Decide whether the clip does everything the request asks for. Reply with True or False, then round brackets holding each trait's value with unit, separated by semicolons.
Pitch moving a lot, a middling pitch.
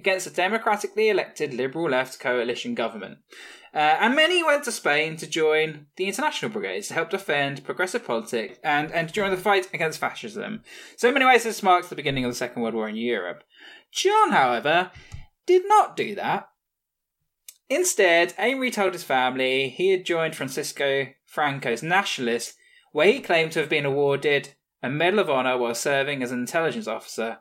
True (7.6 semitones; 165 Hz)